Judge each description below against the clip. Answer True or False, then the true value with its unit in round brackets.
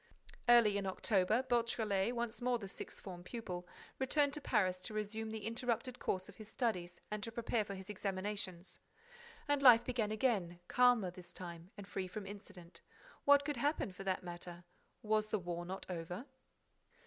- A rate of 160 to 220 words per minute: True (170 wpm)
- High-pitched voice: True (210 Hz)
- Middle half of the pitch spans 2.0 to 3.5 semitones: False (4.3 semitones)